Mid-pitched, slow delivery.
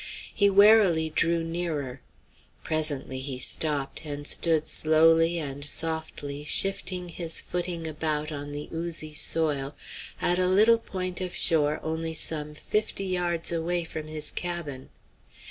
Yes: medium, 160 Hz; slow, 130 wpm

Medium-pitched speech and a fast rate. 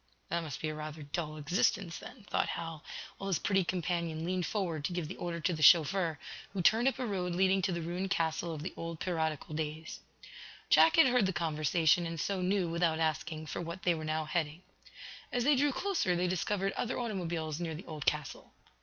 Yes: medium, 170 Hz; fast, 210 wpm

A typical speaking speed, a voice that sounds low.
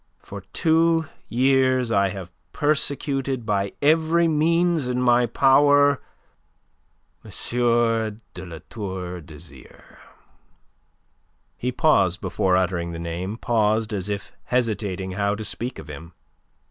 No: slow, 115 wpm; low, 115 Hz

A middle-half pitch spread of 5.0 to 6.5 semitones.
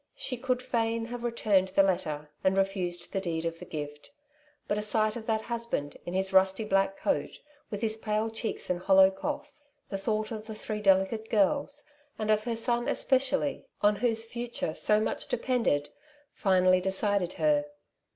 No: average, 3.4 semitones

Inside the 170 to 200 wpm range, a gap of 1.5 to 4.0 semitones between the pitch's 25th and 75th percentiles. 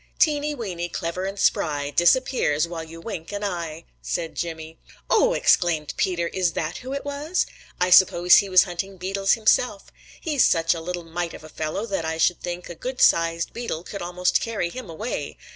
Yes: average, 185 wpm; average, 3.7 semitones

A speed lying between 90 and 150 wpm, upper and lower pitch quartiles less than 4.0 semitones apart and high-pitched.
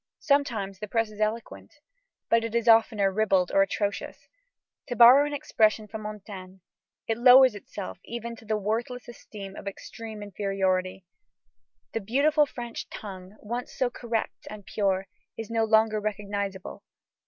Yes: average, 145 wpm; average, 2.7 semitones; high, 215 Hz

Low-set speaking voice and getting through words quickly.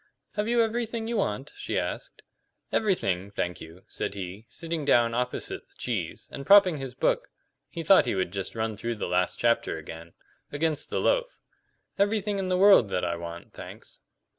No: low, 125 Hz; average, 180 wpm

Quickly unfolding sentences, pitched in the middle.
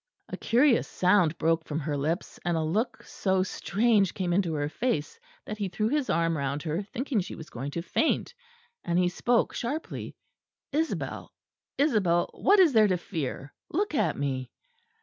No: average, 170 wpm; medium, 180 Hz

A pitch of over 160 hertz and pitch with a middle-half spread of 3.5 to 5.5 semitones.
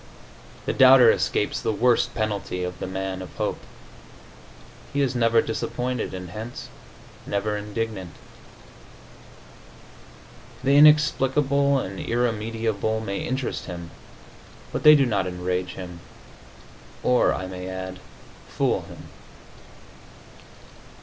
No: low, 110 Hz; average, 5.1 semitones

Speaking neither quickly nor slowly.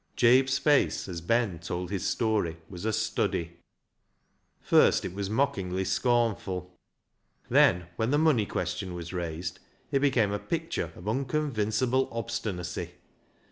No: slow, 130 wpm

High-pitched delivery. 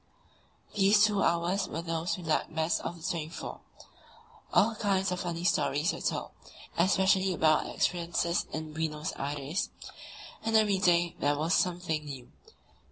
No: medium, 170 Hz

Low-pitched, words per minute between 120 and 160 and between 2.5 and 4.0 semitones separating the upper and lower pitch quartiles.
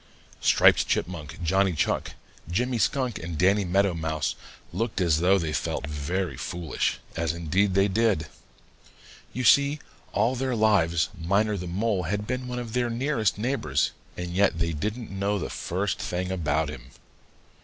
No: very low, 95 Hz; average, 155 wpm; average, 4.8 semitones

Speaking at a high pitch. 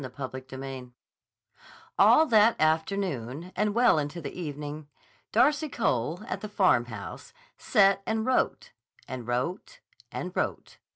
No: medium, 165 Hz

